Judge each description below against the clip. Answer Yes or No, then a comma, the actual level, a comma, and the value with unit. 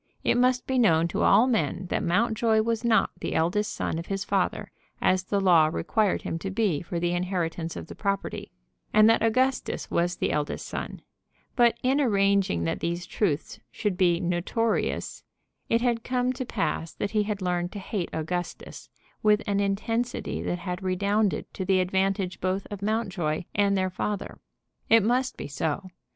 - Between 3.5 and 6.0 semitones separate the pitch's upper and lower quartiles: Yes, average, 4.0 semitones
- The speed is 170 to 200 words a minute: Yes, average, 175 wpm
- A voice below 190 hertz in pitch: No, high, 195 Hz